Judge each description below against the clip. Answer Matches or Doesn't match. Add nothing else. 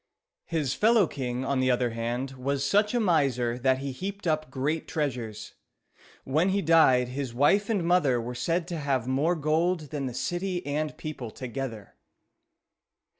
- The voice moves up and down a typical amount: Matches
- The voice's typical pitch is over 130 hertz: Matches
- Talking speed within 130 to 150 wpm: Doesn't match